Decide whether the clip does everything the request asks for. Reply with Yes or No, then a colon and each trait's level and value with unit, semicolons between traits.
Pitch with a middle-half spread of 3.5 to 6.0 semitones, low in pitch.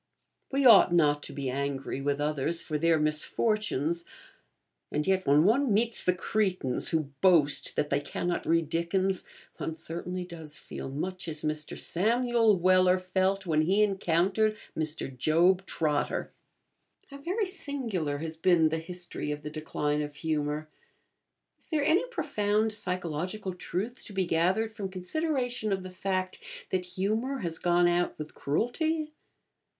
No: average, 5.2 semitones; medium, 180 Hz